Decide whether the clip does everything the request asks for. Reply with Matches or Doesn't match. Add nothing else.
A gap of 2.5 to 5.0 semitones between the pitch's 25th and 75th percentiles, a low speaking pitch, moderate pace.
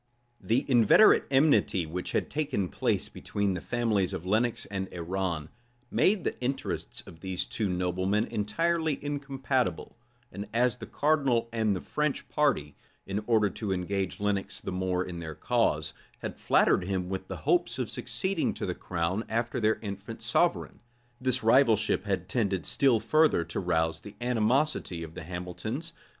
Doesn't match